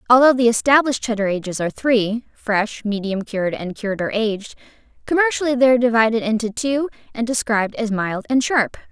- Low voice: No, high, 230 Hz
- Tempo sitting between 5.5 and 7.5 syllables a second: Yes, 6.0 syllables/s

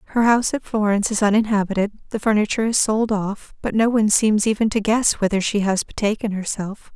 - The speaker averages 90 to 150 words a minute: No, average, 200 wpm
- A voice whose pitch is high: Yes, high, 210 Hz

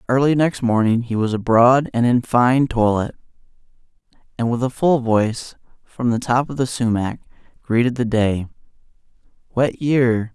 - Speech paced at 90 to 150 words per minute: Yes, average, 145 wpm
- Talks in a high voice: No, low, 120 Hz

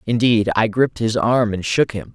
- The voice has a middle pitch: No, low, 110 Hz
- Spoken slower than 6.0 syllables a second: Yes, 5.0 syllables/s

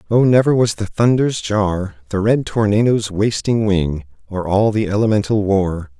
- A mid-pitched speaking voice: No, low, 105 Hz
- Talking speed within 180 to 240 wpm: No, average, 160 wpm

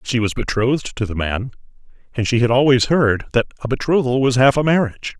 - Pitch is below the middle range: Yes, low, 125 Hz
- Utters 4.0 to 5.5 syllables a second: No, 5.9 syllables/s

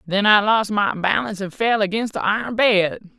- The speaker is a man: No, female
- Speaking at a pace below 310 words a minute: Yes, fast, 205 wpm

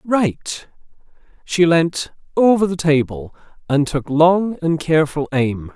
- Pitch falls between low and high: Yes, medium, 160 Hz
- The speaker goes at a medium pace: No, slow, 125 wpm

